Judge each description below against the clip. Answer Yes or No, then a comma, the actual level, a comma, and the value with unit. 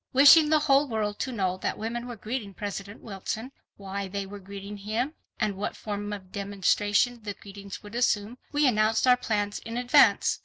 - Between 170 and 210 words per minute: Yes, average, 185 wpm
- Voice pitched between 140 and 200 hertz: No, high, 210 Hz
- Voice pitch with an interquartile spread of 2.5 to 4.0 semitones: Yes, average, 3.3 semitones